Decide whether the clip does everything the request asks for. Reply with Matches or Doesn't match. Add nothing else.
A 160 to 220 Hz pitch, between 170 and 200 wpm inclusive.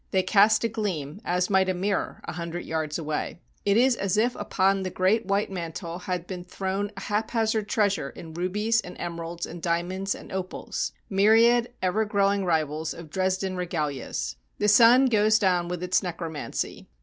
Matches